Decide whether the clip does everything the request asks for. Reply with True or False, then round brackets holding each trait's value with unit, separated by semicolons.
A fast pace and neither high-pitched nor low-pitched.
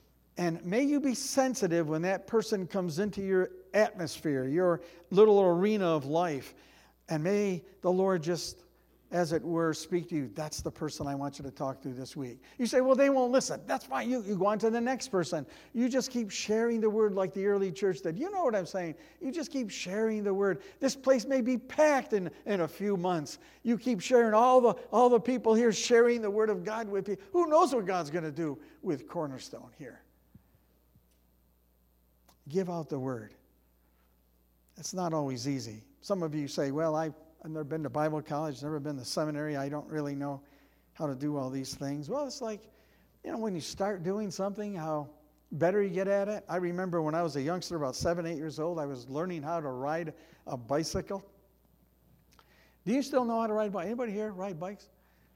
True (210 wpm; 180 Hz)